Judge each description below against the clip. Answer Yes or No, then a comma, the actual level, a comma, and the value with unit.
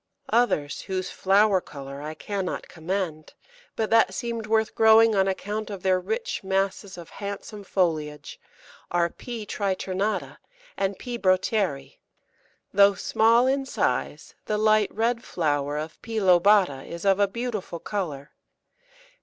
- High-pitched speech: Yes, high, 195 Hz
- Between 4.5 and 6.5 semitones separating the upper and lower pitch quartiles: No, average, 4.0 semitones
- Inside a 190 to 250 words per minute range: No, slow, 135 wpm